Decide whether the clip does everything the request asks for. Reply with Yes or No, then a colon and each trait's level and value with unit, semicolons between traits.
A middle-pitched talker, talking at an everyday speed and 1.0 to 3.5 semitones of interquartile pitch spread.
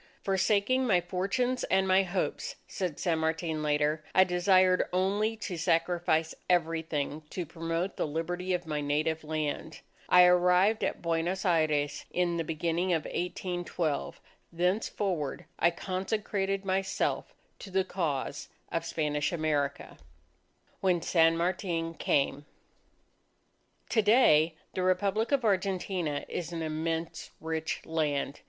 No: medium, 175 Hz; slow, 125 wpm; average, 2.9 semitones